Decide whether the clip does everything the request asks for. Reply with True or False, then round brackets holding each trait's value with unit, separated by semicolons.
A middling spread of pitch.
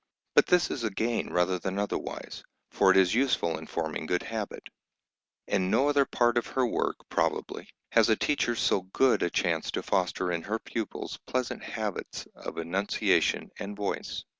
True (4.6 semitones)